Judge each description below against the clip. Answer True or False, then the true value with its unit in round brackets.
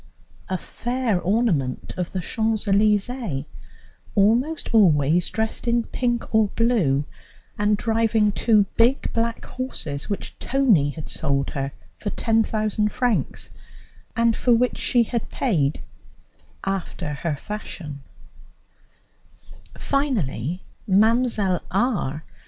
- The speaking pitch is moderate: False (210 Hz)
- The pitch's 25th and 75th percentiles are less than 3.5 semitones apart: False (5.4 semitones)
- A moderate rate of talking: False (105 wpm)